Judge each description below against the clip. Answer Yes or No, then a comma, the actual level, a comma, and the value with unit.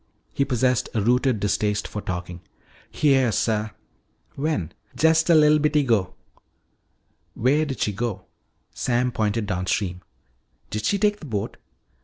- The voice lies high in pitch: No, low, 120 Hz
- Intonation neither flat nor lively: No, wide, 5.9 semitones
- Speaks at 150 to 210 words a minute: No, slow, 135 wpm